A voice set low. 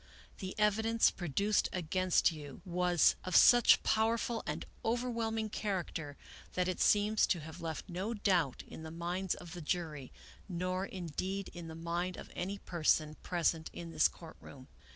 No: medium, 180 Hz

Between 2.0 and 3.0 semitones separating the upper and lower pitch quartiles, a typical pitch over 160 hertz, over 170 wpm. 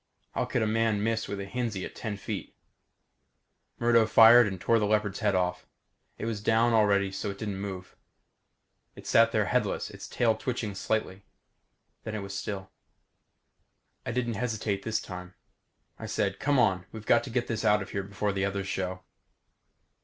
No: narrow, 2.5 semitones; low, 105 Hz; average, 180 wpm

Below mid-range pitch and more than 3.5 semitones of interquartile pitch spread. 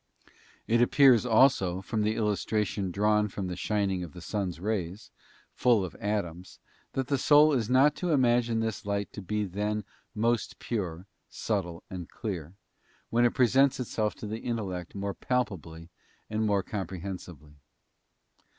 Yes: low, 105 Hz; average, 4.1 semitones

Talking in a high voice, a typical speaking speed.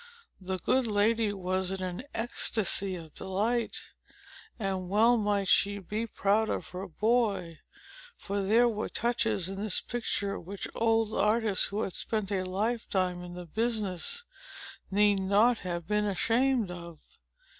Yes: high, 205 Hz; average, 145 wpm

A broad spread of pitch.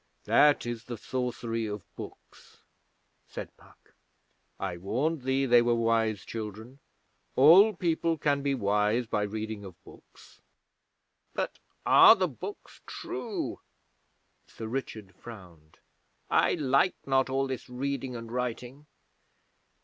No: average, 3.8 semitones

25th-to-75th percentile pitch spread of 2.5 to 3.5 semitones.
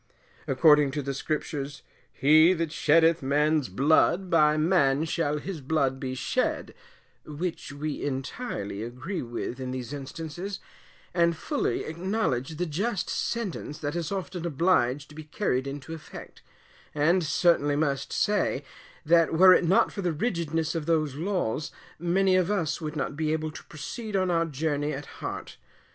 Yes: average, 3.2 semitones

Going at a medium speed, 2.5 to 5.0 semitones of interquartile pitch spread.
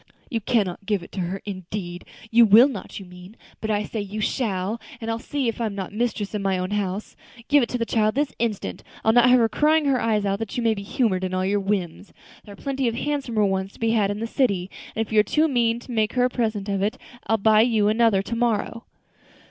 No: fast, 260 wpm; average, 3.0 semitones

